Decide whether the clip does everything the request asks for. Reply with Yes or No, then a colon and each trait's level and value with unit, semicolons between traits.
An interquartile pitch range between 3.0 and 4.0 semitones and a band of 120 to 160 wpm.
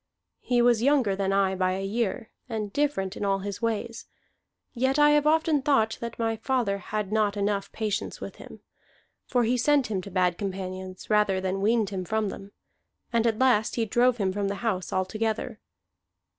No: average, 3.5 semitones; average, 185 wpm